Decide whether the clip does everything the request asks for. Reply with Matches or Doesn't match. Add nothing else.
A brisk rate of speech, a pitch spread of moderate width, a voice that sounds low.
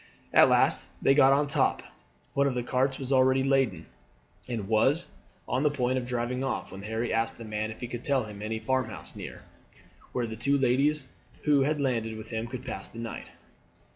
Matches